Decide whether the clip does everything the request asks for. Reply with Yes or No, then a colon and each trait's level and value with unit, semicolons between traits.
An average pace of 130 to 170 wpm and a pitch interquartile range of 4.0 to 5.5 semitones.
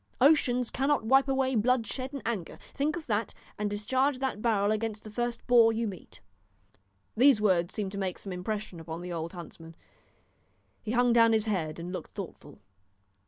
No: average, 180 wpm; average, 4.7 semitones